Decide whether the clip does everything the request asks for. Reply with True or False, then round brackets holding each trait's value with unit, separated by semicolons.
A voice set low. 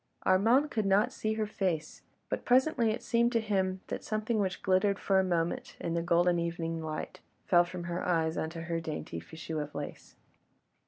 False (185 Hz)